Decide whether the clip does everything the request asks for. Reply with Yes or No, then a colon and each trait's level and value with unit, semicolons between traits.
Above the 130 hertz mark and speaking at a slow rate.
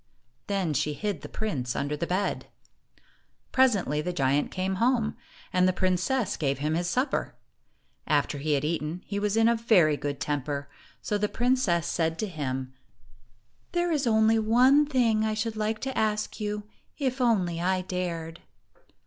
No: high, 190 Hz; average, 165 wpm